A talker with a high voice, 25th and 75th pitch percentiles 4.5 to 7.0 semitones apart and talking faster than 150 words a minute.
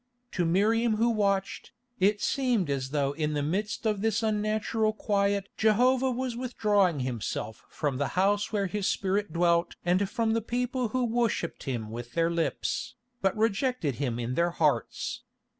Yes: high, 200 Hz; average, 5.2 semitones; average, 160 wpm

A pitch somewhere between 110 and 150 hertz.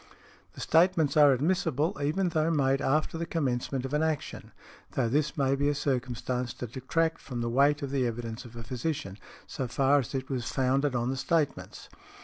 Yes: low, 135 Hz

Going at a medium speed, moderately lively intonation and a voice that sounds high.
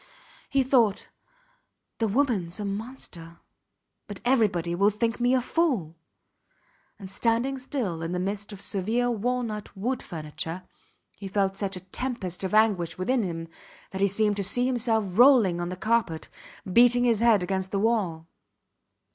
Yes: average, 155 wpm; average, 4.5 semitones; high, 205 Hz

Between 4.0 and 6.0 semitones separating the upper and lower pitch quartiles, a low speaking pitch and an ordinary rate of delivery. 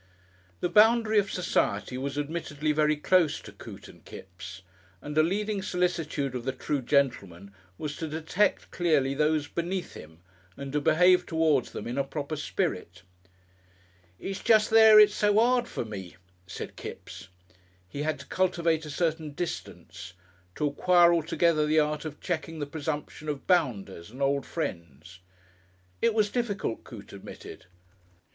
No: average, 4.7 semitones; medium, 155 Hz; average, 150 wpm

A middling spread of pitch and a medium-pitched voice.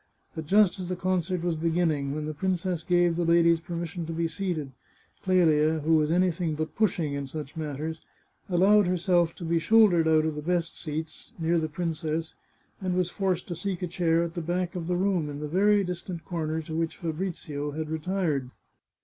No: narrow, 2.3 semitones; medium, 170 Hz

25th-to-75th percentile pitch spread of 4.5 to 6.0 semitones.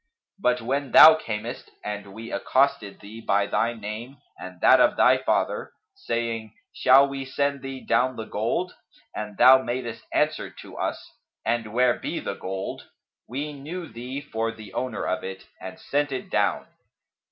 No: average, 3.9 semitones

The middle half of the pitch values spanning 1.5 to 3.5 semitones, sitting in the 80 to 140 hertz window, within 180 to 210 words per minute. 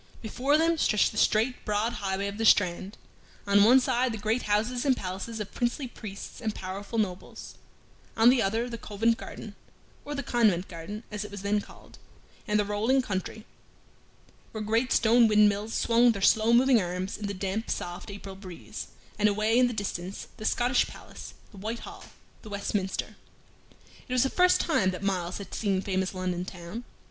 No: average, 3.2 semitones; high, 210 Hz; average, 185 wpm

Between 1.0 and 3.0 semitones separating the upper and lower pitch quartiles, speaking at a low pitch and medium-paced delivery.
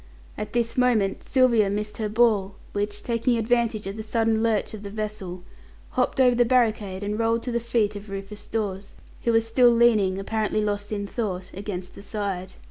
No: narrow, 2.4 semitones; high, 215 Hz; average, 190 wpm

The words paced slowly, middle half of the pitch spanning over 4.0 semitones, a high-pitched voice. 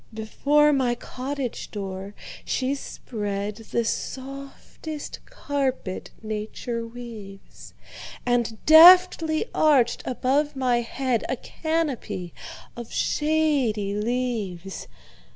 Yes: slow, 75 wpm; average, 4.7 semitones; high, 245 Hz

